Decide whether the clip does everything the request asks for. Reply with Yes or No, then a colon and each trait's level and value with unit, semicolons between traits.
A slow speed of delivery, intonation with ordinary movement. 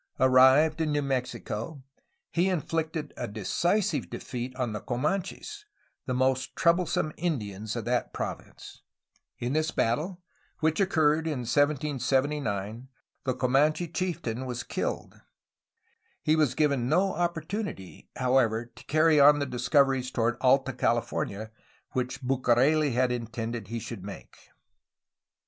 Yes: slow, 125 wpm; average, 4.4 semitones